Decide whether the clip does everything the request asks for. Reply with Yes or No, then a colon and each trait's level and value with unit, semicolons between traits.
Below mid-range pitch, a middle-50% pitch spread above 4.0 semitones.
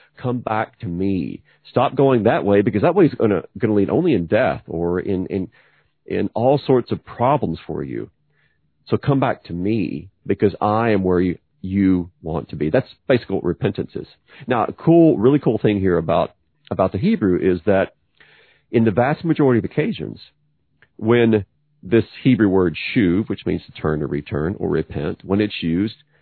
Yes: low, 105 Hz; average, 4.8 semitones